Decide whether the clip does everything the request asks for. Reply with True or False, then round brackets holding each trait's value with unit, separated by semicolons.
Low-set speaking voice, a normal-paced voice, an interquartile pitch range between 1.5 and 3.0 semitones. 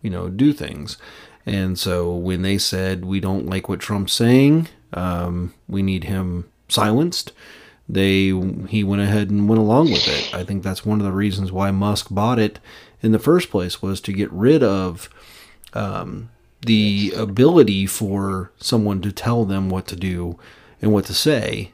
True (100 Hz; 175 wpm; 2.7 semitones)